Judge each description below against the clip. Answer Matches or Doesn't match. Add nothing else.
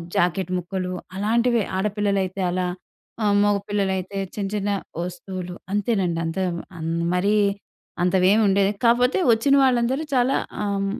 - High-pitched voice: Matches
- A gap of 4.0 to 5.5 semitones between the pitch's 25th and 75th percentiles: Doesn't match